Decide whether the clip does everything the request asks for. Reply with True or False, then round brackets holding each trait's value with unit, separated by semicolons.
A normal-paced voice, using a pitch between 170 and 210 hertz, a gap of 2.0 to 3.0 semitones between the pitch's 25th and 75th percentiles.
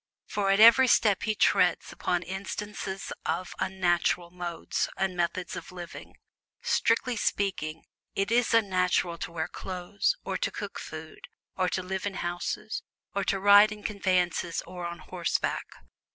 True (150 wpm; 190 Hz; 2.6 semitones)